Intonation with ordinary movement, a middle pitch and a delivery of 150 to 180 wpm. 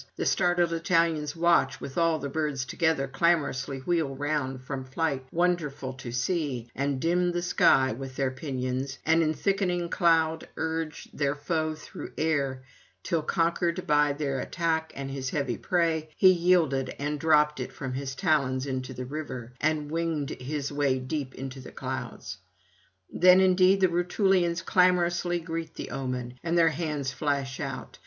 Yes: average, 3.9 semitones; medium, 150 Hz; average, 160 wpm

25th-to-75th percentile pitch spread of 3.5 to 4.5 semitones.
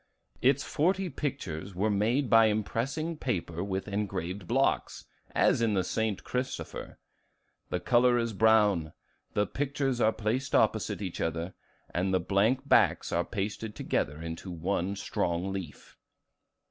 No: average, 5.1 semitones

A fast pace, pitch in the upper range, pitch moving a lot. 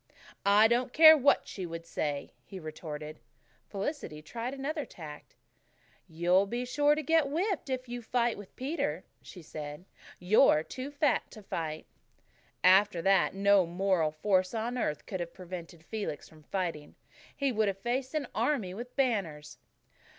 No: average, 155 wpm; high, 200 Hz; wide, 7.1 semitones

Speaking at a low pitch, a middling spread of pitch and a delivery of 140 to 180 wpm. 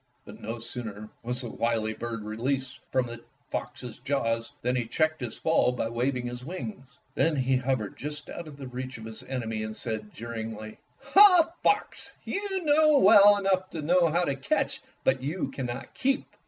No: low, 130 Hz; wide, 5.8 semitones; average, 170 wpm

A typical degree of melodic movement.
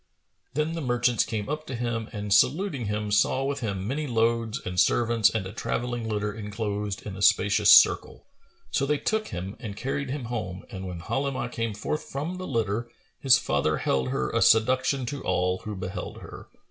Yes: average, 4.6 semitones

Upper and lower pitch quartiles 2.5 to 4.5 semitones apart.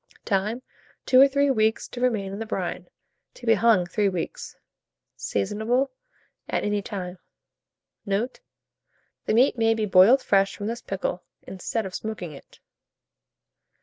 Yes: average, 3.3 semitones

